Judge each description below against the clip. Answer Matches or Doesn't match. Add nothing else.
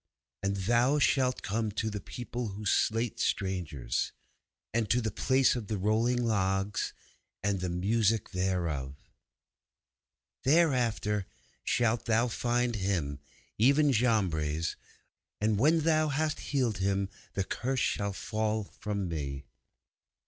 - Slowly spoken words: Matches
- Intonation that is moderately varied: Matches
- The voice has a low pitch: Matches